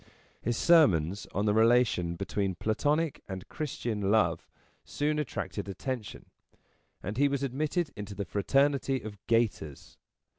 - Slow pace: Yes, slow, 125 wpm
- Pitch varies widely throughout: Yes, wide, 5.8 semitones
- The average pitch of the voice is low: Yes, low, 110 Hz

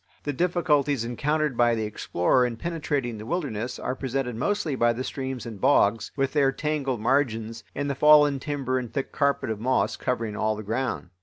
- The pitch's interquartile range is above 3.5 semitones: Yes, average, 3.9 semitones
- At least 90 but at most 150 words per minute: No, average, 185 wpm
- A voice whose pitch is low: Yes, low, 130 Hz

